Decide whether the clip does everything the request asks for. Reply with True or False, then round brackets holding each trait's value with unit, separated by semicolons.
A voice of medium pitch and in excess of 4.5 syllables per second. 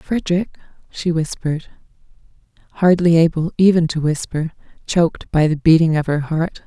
True (165 Hz; 5.1 syllables/s)